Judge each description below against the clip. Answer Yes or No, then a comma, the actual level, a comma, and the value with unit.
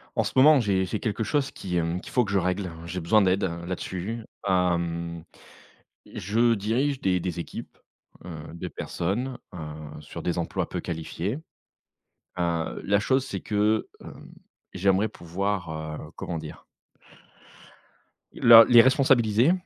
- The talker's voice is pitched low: Yes, very low, 95 Hz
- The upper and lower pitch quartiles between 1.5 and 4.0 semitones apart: No, average, 4.7 semitones